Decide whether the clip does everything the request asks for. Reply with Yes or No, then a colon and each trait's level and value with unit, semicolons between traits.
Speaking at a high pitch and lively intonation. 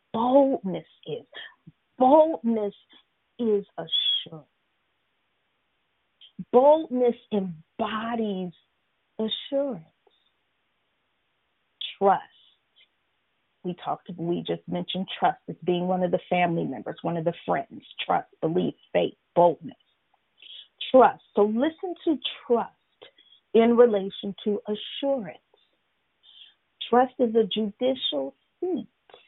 Yes: high, 220 Hz; wide, 6.4 semitones